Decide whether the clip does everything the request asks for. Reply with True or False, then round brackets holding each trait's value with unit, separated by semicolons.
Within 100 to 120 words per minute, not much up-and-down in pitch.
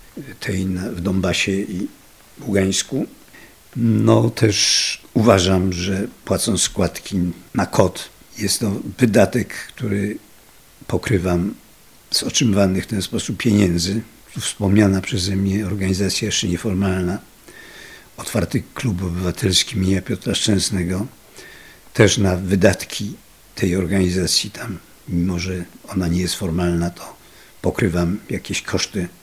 True (115 wpm; 2.0 semitones)